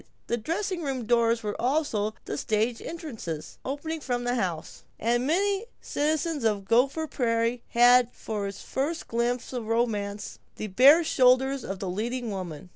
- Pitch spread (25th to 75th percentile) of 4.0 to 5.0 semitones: Yes, average, 4.4 semitones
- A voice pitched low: No, high, 240 Hz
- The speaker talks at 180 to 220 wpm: No, average, 160 wpm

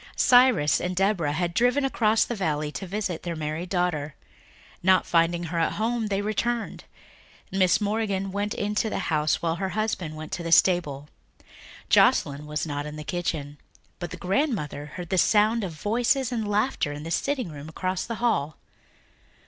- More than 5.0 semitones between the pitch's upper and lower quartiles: Yes, wide, 5.5 semitones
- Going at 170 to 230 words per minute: Yes, average, 175 wpm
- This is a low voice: No, medium, 180 Hz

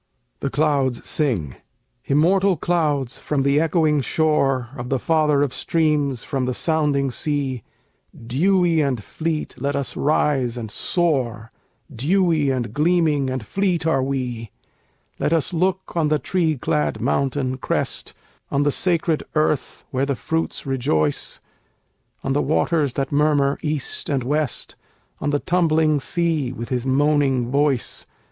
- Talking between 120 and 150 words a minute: Yes, average, 140 wpm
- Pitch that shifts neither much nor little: Yes, average, 3.3 semitones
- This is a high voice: No, medium, 145 Hz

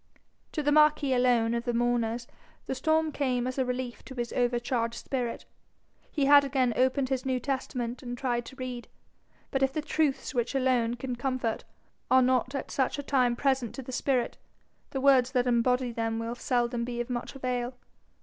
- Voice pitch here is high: Yes, very high, 255 Hz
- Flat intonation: Yes, narrow, 1.9 semitones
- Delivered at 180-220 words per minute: Yes, average, 190 wpm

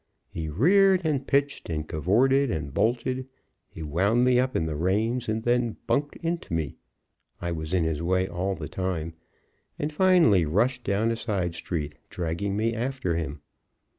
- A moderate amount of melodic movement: No, wide, 7.4 semitones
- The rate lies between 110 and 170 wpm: Yes, average, 165 wpm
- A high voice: No, low, 100 Hz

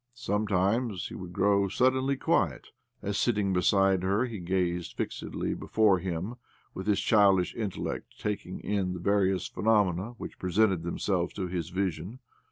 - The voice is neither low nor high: No, very low, 95 Hz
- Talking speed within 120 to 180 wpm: Yes, average, 150 wpm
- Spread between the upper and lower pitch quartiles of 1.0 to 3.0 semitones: Yes, narrow, 2.5 semitones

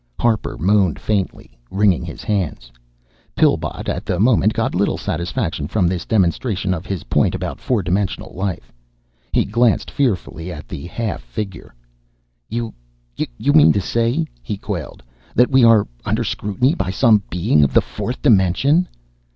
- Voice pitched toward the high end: No, low, 100 Hz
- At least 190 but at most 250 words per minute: No, average, 150 wpm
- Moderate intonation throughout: Yes, average, 4.7 semitones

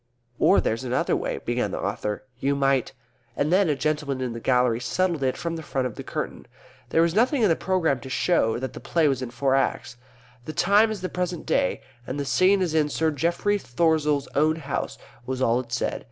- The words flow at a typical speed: No, fast, 225 wpm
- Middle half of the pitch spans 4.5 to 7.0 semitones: Yes, average, 4.8 semitones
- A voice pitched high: No, medium, 145 Hz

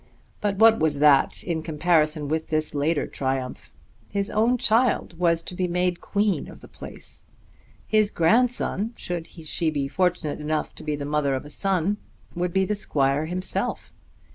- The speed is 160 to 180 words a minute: Yes, average, 165 wpm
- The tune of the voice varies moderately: Yes, average, 4.6 semitones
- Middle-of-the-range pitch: Yes, medium, 170 Hz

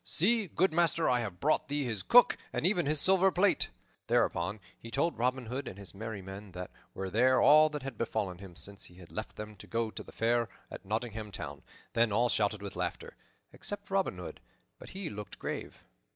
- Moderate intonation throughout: No, wide, 7.2 semitones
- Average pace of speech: No, fast, 210 wpm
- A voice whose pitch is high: No, low, 115 Hz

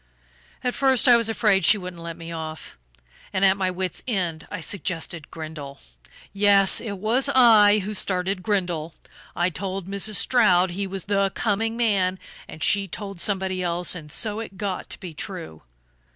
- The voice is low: No, high, 190 Hz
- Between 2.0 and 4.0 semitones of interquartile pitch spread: Yes, average, 3.1 semitones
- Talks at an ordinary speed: Yes, average, 170 wpm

